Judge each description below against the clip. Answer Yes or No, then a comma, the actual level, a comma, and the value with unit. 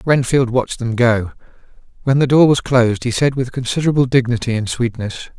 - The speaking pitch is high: No, low, 125 Hz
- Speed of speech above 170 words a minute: Yes, average, 180 wpm